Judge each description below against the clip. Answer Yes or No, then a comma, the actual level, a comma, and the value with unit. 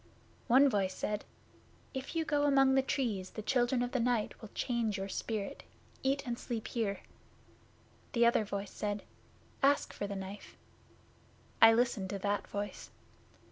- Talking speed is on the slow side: No, average, 155 wpm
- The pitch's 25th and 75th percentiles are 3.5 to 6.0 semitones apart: Yes, average, 4.3 semitones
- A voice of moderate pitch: No, high, 230 Hz